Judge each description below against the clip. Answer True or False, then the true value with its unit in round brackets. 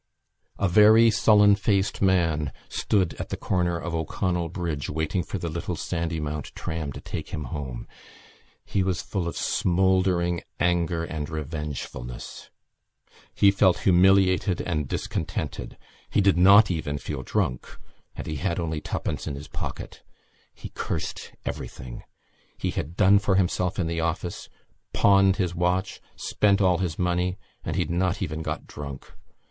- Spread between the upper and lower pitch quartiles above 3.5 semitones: False (3.2 semitones)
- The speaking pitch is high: False (90 Hz)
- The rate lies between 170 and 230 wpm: False (150 wpm)